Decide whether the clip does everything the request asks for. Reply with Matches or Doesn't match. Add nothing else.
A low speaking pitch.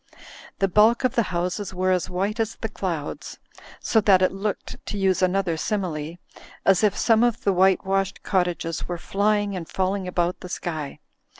Doesn't match